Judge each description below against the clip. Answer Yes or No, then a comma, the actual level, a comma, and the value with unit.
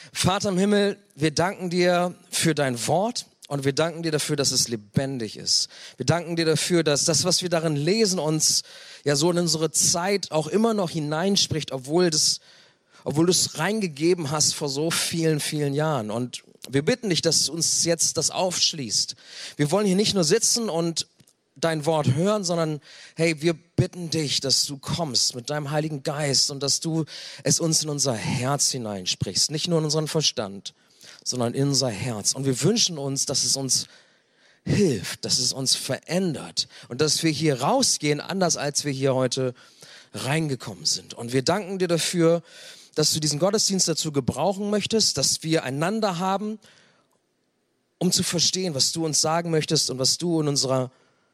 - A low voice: No, medium, 155 Hz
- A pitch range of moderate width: Yes, average, 3.8 semitones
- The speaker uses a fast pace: No, average, 180 wpm